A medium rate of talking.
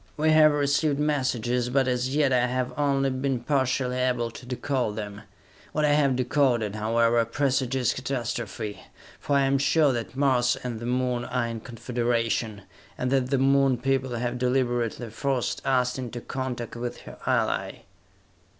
Yes: average, 160 wpm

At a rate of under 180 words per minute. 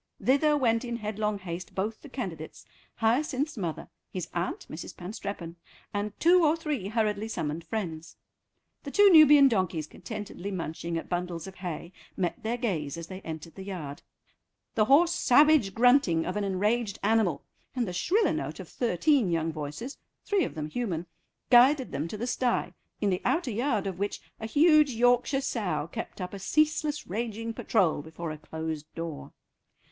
Yes: average, 170 wpm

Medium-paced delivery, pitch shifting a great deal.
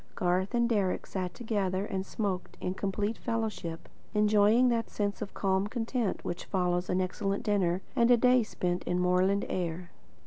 No: average, 165 wpm; average, 3.3 semitones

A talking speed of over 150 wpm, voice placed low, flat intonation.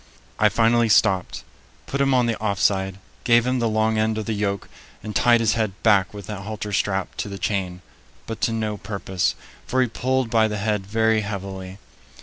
Yes: average, 200 wpm; low, 110 Hz; narrow, 2.3 semitones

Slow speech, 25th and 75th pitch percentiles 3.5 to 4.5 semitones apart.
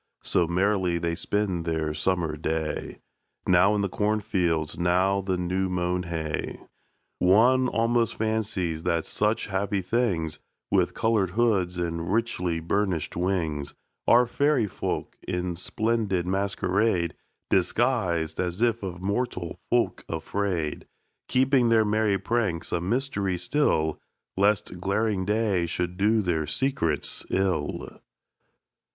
Yes: slow, 120 wpm; average, 4.0 semitones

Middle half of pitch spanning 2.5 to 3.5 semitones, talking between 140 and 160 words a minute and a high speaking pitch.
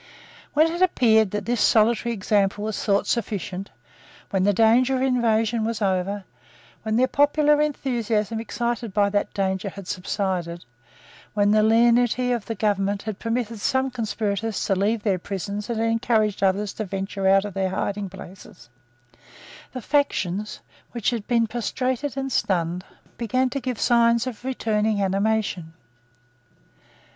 Yes: average, 3.2 semitones; average, 145 wpm; high, 215 Hz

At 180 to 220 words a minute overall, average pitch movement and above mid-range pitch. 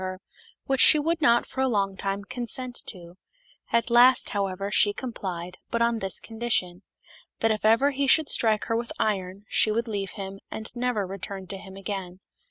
Yes: average, 190 wpm; average, 3.6 semitones; high, 215 Hz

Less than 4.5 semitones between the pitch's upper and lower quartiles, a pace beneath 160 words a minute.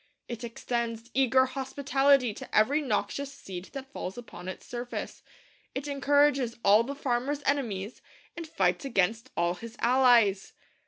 Yes: average, 3.8 semitones; average, 140 wpm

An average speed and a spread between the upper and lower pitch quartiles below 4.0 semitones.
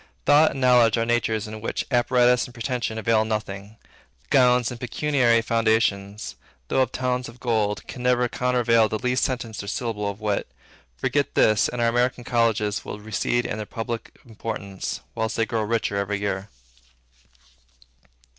Yes: average, 160 wpm; narrow, 2.4 semitones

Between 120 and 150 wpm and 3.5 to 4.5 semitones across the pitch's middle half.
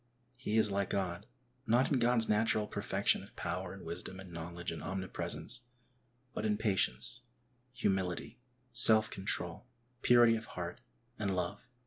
Yes: average, 140 wpm; average, 4.1 semitones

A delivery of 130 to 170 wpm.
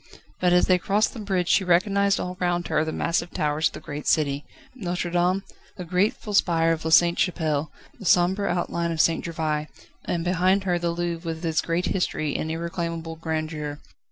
No: average, 190 wpm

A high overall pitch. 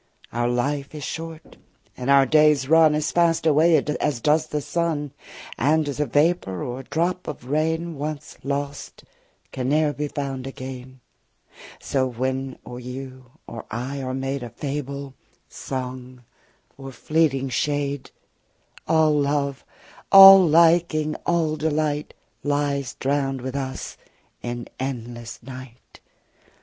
No: medium, 140 Hz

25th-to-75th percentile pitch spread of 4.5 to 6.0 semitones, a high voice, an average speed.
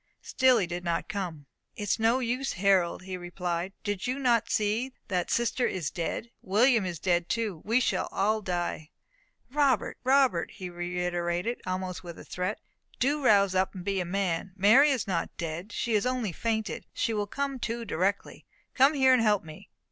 Yes: average, 5.0 semitones; high, 200 Hz; average, 185 wpm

